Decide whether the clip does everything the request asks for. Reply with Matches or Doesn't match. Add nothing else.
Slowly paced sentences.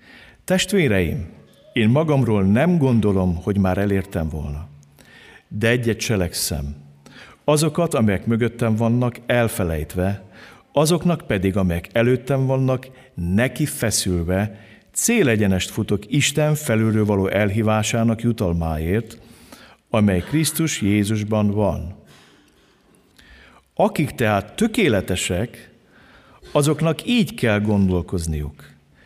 Matches